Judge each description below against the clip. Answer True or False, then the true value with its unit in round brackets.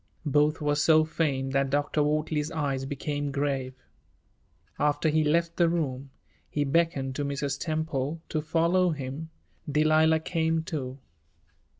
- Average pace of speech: False (130 wpm)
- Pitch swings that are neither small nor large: False (2.3 semitones)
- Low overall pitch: False (150 Hz)